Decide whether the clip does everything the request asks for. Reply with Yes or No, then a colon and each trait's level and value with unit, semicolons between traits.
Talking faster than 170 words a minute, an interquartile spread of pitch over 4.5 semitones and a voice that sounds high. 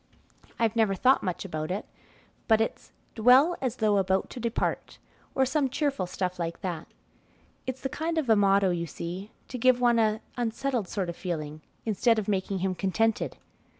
Yes: average, 180 wpm; average, 4.9 semitones; high, 215 Hz